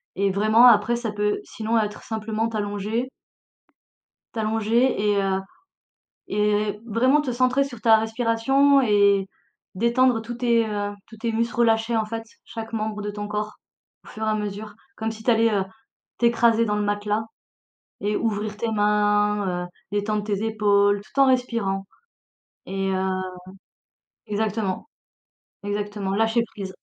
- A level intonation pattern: Yes, narrow, 1.9 semitones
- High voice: Yes, high, 215 Hz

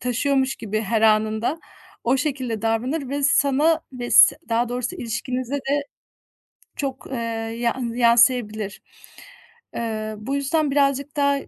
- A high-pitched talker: Yes, very high, 250 Hz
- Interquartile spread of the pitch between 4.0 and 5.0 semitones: No, average, 3.5 semitones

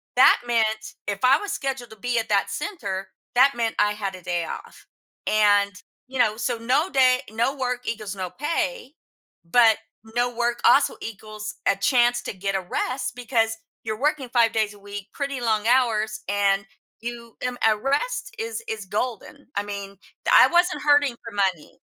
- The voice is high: Yes, high, 230 Hz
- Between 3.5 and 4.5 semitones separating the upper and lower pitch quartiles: Yes, average, 3.8 semitones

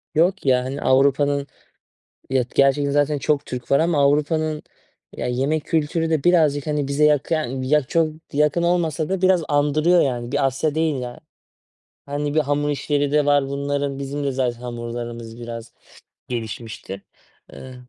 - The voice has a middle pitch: Yes, medium, 145 Hz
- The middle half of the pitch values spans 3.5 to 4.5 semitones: No, narrow, 2.6 semitones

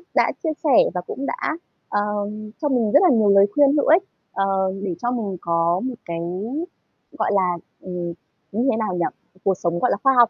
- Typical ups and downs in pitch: No, wide, 5.7 semitones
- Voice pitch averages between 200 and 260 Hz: Yes, high, 210 Hz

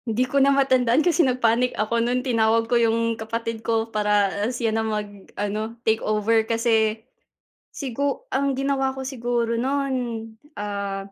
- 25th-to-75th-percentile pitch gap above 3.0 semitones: No, average, 2.7 semitones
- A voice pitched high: Yes, high, 230 Hz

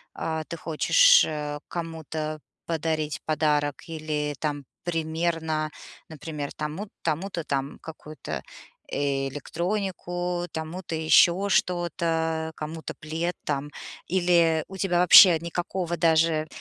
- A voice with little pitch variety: Yes, narrow, 2.0 semitones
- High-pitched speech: No, medium, 160 Hz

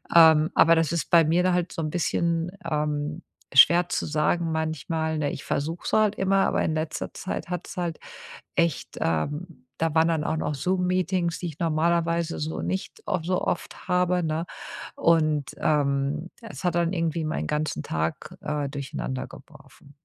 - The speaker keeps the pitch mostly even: Yes, narrow, 2.3 semitones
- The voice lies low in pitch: No, medium, 165 Hz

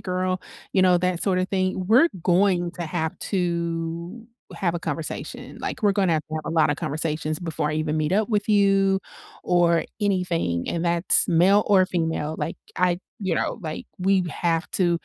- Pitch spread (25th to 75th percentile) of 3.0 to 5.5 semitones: No, narrow, 2.6 semitones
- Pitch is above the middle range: No, medium, 175 Hz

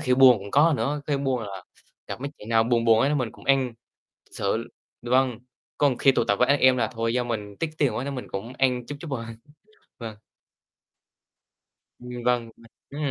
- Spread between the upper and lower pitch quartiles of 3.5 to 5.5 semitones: No, average, 3.0 semitones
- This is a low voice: Yes, low, 125 Hz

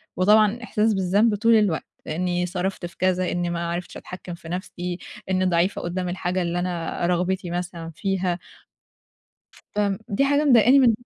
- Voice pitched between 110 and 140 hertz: No, medium, 185 Hz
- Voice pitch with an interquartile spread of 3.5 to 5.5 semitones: No, average, 2.7 semitones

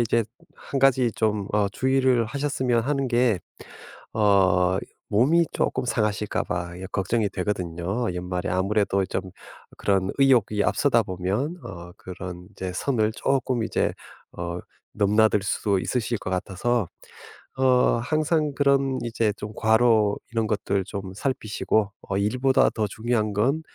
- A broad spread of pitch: No, average, 4.6 semitones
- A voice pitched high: No, low, 110 Hz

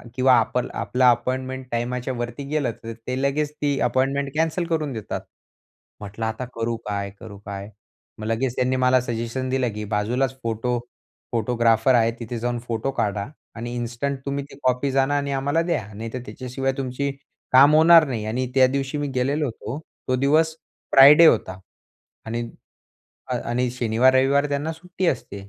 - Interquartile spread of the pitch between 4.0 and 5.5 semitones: No, average, 3.1 semitones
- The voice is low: Yes, low, 130 Hz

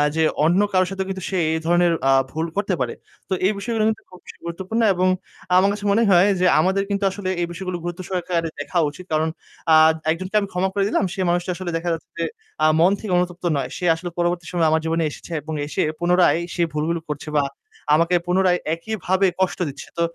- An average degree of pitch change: No, narrow, 2.1 semitones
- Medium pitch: Yes, medium, 180 Hz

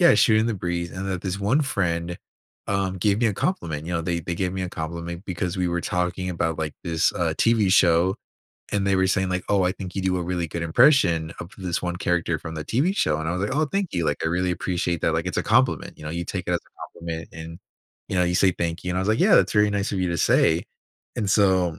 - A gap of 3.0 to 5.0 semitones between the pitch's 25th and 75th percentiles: No, narrow, 2.5 semitones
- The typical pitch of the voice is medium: No, very low, 90 Hz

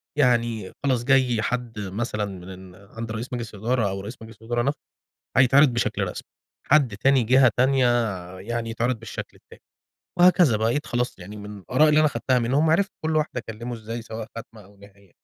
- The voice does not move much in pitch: No, average, 3.4 semitones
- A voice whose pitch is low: Yes, low, 120 Hz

